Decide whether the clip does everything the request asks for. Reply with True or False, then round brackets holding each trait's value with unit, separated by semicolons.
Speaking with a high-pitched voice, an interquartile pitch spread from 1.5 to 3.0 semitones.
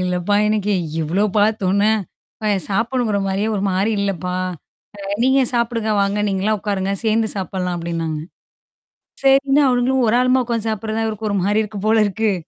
True (210 Hz; 2.7 semitones)